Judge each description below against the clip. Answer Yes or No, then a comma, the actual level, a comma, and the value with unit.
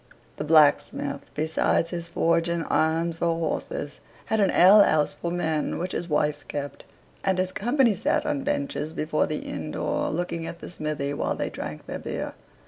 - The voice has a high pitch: No, medium, 165 Hz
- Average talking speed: Yes, average, 180 wpm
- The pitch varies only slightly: No, average, 3.2 semitones